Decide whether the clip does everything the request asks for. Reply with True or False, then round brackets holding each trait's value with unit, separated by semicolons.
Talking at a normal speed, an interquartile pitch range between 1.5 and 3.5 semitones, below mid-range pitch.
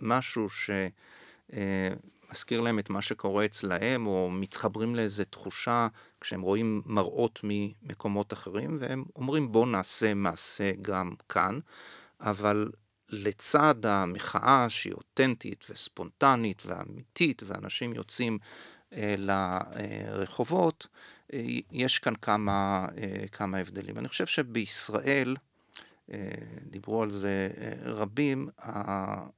True (110 wpm; 3.0 semitones; 105 Hz)